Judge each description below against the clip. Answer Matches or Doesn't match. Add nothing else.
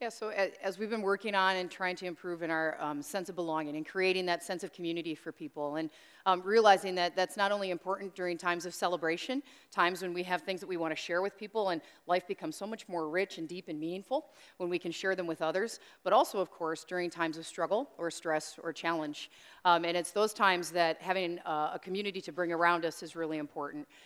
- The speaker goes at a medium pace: Doesn't match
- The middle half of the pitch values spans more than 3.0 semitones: Doesn't match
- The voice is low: Doesn't match